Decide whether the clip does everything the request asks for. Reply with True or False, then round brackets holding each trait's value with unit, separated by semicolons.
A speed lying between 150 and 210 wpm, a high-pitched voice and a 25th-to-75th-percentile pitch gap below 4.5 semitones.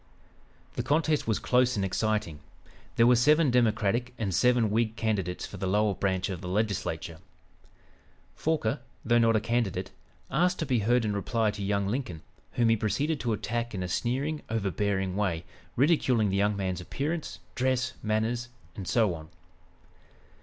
False (160 wpm; 110 Hz; 4.0 semitones)